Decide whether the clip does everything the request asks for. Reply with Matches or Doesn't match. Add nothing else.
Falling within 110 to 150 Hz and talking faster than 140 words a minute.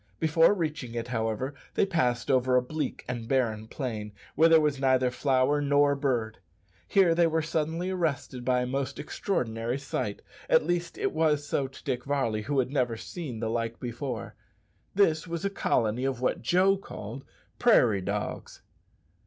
Matches